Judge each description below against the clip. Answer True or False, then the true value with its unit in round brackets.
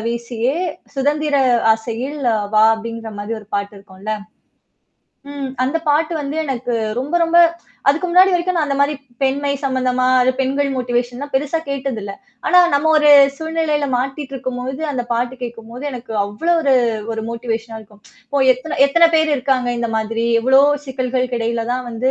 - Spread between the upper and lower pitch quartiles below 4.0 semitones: True (3.6 semitones)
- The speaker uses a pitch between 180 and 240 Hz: False (260 Hz)